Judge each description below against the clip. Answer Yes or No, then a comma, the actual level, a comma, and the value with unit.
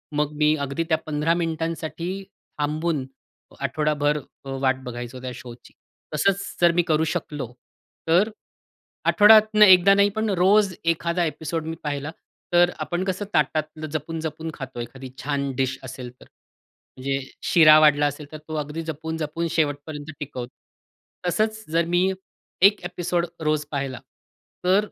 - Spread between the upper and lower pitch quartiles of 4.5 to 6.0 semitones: No, average, 3.3 semitones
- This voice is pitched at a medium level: Yes, medium, 155 Hz